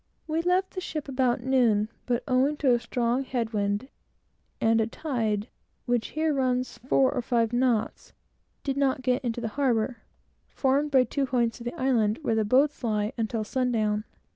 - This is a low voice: No, very high, 250 Hz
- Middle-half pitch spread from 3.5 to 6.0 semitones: No, average, 3.0 semitones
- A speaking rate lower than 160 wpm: No, average, 175 wpm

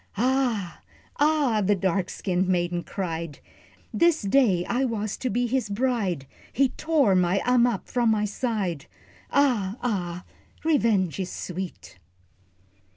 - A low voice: No, high, 210 Hz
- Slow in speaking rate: Yes, slow, 125 wpm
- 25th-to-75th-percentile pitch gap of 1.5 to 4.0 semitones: No, wide, 5.5 semitones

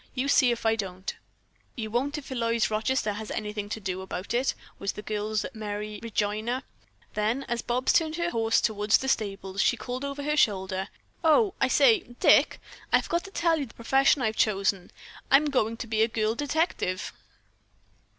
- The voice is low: No, high, 225 Hz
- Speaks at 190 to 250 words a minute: No, average, 180 wpm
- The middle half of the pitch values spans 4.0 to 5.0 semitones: Yes, average, 4.4 semitones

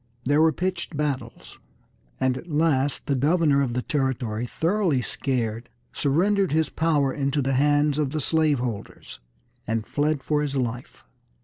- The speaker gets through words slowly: No, average, 150 wpm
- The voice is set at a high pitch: No, medium, 145 Hz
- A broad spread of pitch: No, average, 3.2 semitones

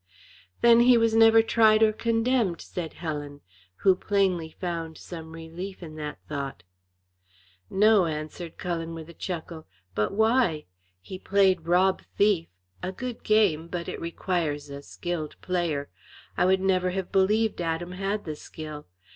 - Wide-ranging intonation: No, average, 4.0 semitones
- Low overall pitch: No, medium, 180 Hz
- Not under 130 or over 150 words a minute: Yes, average, 145 wpm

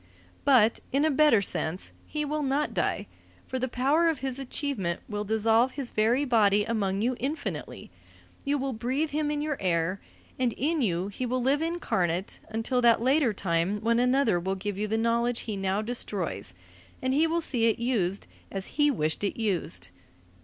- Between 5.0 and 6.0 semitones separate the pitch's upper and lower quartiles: Yes, average, 5.3 semitones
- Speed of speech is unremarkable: Yes, average, 180 wpm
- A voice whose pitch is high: Yes, high, 235 Hz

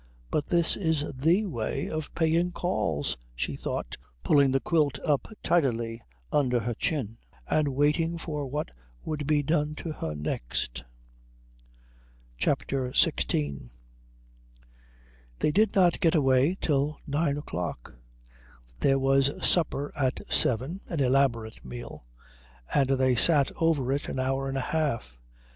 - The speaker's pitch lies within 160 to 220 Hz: No, medium, 140 Hz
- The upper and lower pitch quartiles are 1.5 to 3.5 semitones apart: No, average, 3.9 semitones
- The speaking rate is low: Yes, slow, 130 wpm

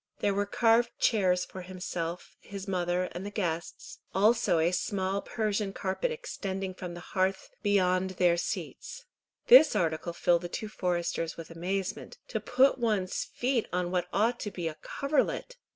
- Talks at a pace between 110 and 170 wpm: Yes, average, 160 wpm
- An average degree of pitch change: Yes, average, 3.4 semitones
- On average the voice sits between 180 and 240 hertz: Yes, high, 190 Hz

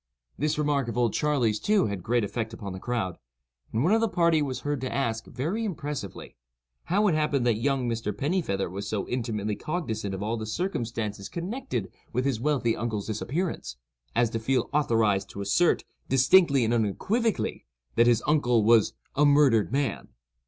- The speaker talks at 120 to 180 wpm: Yes, average, 175 wpm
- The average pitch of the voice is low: Yes, low, 120 Hz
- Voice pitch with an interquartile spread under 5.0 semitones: No, average, 5.3 semitones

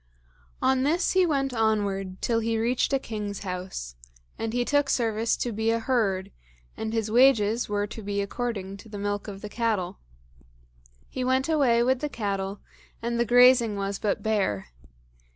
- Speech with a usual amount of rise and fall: Yes, average, 3.3 semitones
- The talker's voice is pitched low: No, high, 225 Hz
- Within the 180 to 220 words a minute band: No, average, 170 wpm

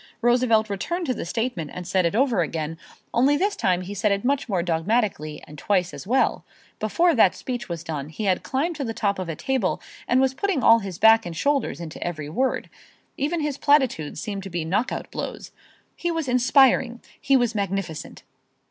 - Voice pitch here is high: Yes, high, 220 Hz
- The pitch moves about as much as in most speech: No, wide, 6.8 semitones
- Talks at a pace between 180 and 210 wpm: Yes, average, 200 wpm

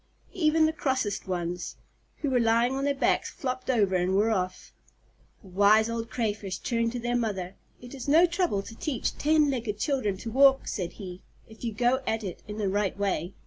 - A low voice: No, high, 225 Hz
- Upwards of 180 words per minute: Yes, average, 200 wpm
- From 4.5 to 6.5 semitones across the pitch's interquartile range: Yes, average, 4.8 semitones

